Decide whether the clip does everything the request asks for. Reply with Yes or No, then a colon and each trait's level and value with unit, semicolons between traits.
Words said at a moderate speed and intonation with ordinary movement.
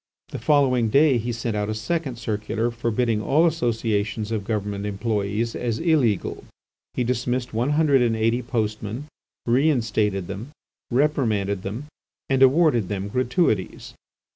No: slow, 130 wpm; average, 3.7 semitones